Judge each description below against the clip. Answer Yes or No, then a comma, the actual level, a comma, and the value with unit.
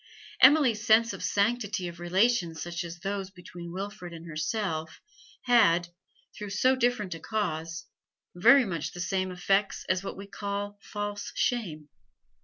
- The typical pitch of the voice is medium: No, high, 195 Hz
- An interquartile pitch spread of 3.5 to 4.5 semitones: Yes, average, 3.8 semitones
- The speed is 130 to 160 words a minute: Yes, average, 150 wpm